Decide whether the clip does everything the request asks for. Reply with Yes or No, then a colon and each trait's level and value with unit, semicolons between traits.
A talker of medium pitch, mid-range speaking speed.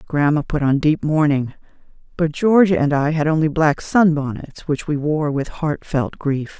Yes: medium, 150 Hz; average, 180 wpm